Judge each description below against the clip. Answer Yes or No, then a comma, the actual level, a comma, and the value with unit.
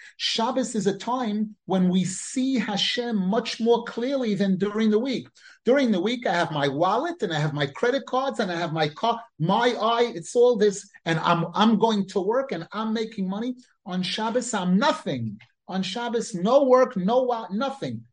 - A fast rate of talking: No, average, 195 wpm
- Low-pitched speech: No, high, 215 Hz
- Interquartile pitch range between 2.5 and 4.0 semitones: No, average, 4.6 semitones